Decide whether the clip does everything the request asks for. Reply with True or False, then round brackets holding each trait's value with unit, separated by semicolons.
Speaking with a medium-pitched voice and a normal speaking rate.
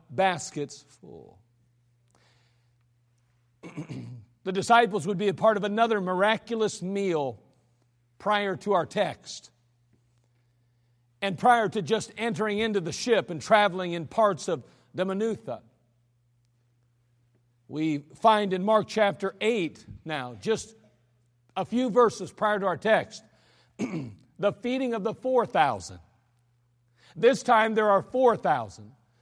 False (155 Hz; 115 wpm)